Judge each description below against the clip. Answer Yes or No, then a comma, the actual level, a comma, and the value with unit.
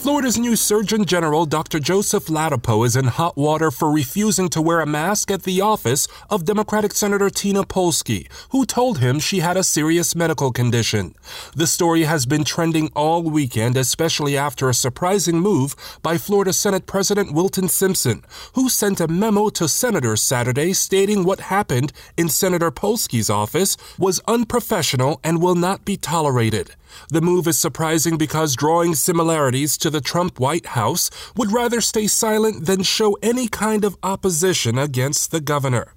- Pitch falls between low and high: Yes, medium, 170 Hz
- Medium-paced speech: Yes, average, 165 wpm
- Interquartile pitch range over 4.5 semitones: Yes, average, 5.1 semitones